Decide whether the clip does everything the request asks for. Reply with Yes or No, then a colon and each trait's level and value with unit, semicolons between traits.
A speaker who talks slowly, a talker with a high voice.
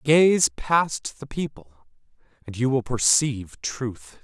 No: slow, 130 wpm; low, 130 Hz